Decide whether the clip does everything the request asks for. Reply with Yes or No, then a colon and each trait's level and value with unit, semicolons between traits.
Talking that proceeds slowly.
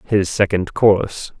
Yes: slow, 130 wpm